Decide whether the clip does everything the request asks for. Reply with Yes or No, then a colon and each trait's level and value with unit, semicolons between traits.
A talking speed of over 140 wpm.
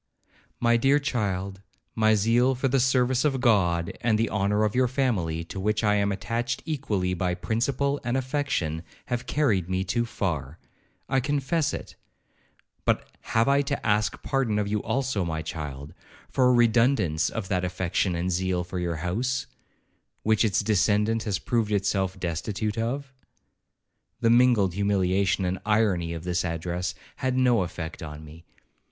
Yes: average, 160 wpm